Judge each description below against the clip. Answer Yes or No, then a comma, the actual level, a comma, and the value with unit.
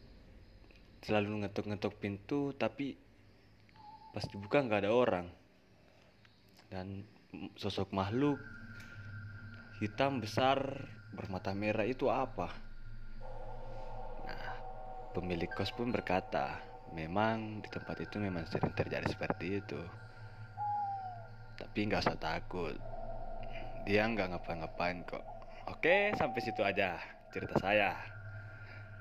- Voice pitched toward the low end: Yes, low, 110 Hz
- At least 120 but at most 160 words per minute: No, average, 95 wpm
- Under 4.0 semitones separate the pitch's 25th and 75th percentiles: Yes, average, 3.0 semitones